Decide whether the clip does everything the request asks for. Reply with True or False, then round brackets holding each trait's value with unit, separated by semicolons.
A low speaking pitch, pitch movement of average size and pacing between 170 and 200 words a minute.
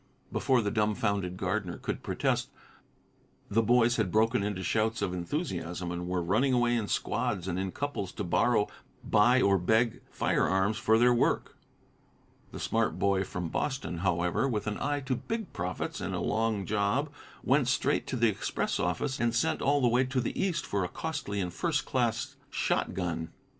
True (110 Hz; 4.6 semitones; 175 wpm)